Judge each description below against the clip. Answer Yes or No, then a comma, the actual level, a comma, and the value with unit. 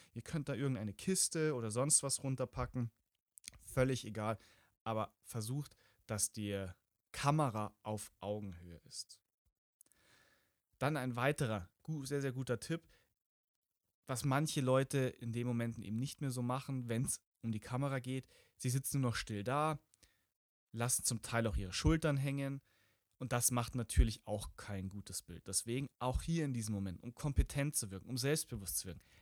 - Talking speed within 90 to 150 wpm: No, average, 160 wpm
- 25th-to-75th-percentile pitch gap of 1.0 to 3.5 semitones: No, average, 4.5 semitones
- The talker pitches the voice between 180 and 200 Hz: No, low, 120 Hz